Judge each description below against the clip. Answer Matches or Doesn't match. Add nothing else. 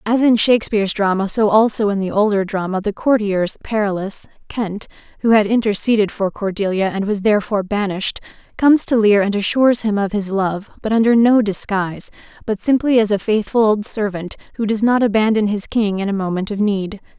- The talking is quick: Doesn't match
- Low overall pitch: Doesn't match